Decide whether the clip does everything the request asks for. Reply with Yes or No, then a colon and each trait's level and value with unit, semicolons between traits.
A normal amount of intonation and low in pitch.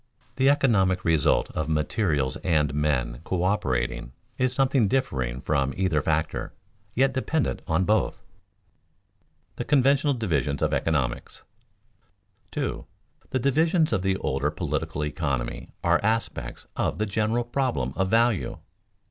No: wide, 8.5 semitones; very low, 95 Hz